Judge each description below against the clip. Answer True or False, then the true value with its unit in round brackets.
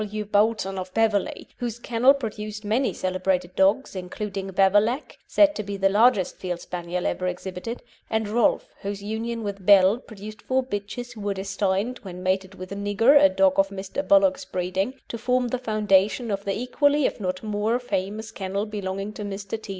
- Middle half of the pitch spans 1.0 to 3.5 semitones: True (2.9 semitones)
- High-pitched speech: True (205 Hz)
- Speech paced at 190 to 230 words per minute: False (180 wpm)